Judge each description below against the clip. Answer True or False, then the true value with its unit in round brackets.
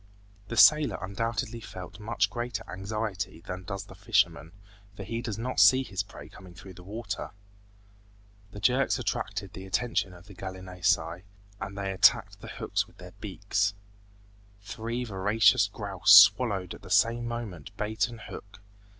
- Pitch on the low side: True (100 Hz)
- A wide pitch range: False (3.3 semitones)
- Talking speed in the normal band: True (155 wpm)